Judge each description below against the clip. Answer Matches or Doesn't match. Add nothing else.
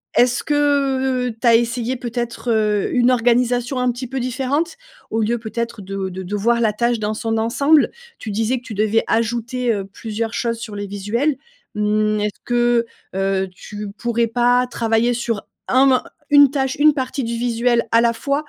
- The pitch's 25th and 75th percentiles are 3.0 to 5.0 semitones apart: Doesn't match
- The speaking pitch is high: Matches